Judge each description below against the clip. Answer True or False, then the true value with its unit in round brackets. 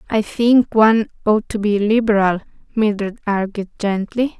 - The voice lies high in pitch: True (215 Hz)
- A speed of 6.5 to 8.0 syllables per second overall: False (4.5 syllables/s)